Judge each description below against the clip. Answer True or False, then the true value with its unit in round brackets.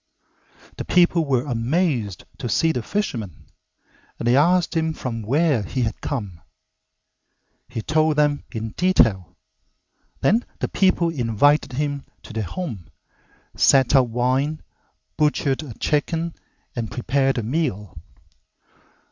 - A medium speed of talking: False (125 wpm)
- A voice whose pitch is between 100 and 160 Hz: True (135 Hz)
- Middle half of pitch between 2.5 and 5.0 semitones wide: False (5.6 semitones)